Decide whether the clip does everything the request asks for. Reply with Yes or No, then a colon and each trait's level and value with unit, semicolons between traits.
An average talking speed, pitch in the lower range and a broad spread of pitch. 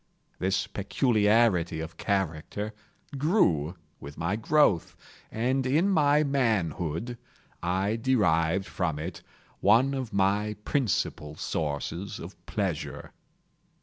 No: slow, 100 wpm; low, 100 Hz; wide, 6.6 semitones